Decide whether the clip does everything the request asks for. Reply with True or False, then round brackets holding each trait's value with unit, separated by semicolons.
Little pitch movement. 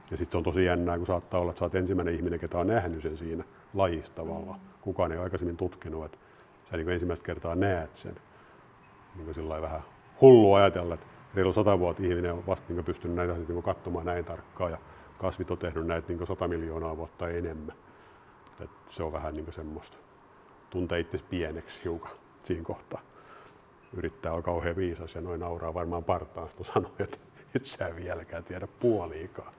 True (1.8 semitones)